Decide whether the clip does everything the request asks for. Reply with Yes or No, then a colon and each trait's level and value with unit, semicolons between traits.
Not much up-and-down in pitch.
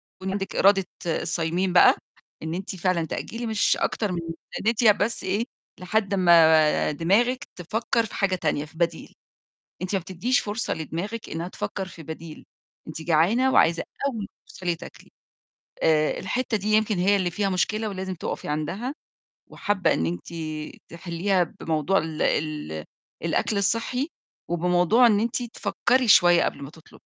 No: average, 4.4 semitones